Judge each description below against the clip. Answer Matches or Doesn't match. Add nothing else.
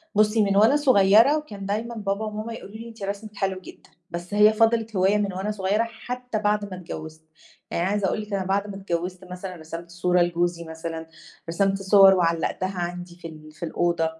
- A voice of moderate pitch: Doesn't match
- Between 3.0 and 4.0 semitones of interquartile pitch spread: Matches